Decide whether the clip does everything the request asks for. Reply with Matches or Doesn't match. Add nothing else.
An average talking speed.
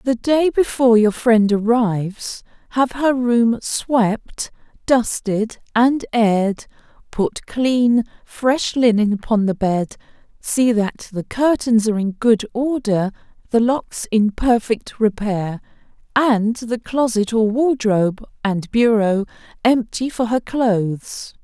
Doesn't match